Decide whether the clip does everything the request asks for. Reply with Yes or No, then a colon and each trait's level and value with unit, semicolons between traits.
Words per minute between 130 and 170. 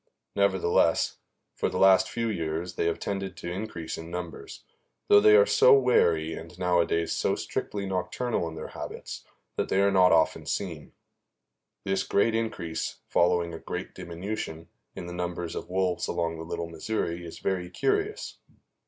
Yes: average, 160 wpm